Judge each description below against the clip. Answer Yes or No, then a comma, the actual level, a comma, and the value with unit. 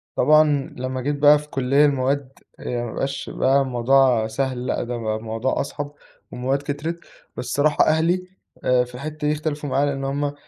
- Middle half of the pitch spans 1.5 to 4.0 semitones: Yes, narrow, 2.5 semitones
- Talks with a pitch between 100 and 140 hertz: Yes, low, 135 Hz